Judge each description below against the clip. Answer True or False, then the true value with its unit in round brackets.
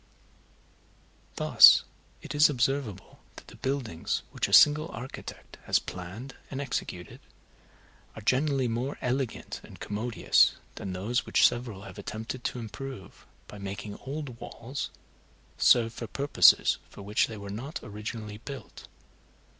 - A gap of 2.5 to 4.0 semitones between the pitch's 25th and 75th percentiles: False (4.4 semitones)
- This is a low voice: True (120 Hz)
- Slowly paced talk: True (130 wpm)